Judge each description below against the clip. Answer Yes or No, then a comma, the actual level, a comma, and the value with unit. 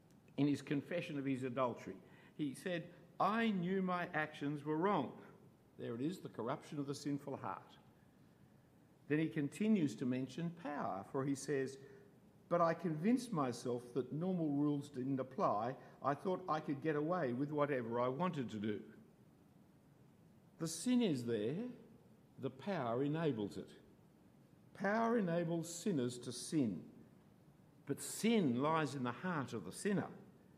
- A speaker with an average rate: Yes, average, 145 wpm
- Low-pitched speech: No, medium, 150 Hz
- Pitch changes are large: No, average, 4.4 semitones